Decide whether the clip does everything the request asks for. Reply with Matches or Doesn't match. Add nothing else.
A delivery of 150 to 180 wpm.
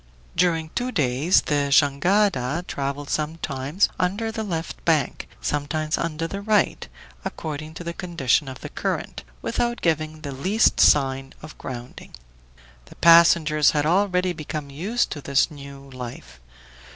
Doesn't match